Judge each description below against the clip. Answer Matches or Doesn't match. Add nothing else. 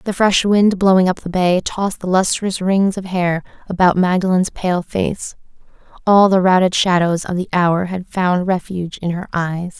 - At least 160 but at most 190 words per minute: Matches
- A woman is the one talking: Matches